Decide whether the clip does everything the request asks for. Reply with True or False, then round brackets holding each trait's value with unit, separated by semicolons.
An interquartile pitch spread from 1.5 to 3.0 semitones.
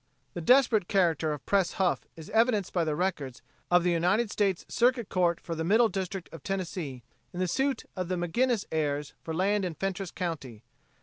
False (3.7 semitones)